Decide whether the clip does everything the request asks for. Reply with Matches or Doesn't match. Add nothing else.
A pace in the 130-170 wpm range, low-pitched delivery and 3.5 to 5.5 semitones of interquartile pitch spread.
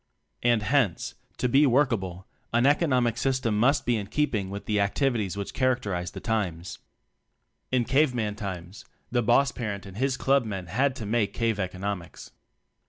Matches